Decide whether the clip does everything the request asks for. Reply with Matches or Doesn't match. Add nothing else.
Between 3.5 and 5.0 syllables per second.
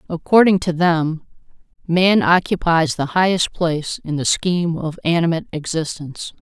Matches